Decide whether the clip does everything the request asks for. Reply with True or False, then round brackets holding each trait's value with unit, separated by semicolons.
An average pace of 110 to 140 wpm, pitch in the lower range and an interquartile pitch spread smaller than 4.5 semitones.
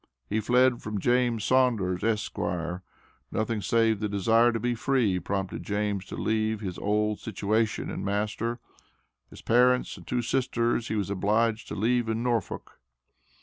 False (150 wpm; 110 Hz; 2.5 semitones)